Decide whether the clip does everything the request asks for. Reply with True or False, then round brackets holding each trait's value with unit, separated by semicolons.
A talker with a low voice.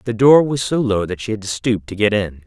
True (110 Hz)